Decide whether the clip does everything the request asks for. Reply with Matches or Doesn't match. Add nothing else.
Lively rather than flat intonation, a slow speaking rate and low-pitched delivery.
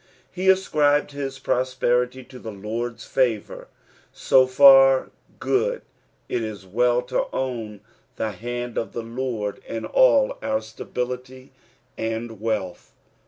Doesn't match